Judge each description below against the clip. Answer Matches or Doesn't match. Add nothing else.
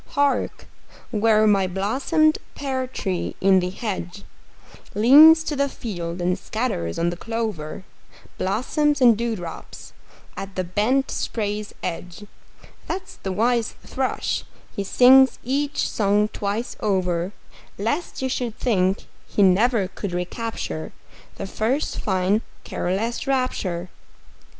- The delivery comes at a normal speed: Doesn't match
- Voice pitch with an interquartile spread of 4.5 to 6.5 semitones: Matches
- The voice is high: Matches